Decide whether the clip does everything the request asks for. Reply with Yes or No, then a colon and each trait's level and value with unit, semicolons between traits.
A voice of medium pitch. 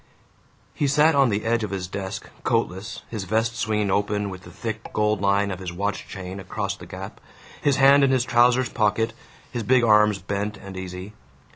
No: low, 105 Hz